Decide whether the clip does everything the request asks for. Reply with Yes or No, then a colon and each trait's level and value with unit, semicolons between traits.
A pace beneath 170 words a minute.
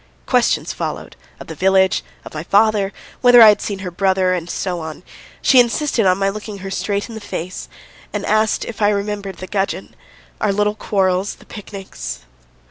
No: average, 185 wpm